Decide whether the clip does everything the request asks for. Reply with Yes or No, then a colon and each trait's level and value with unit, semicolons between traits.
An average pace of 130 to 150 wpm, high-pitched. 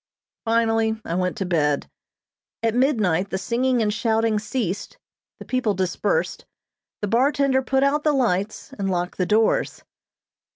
Yes: average, 140 wpm; high, 220 Hz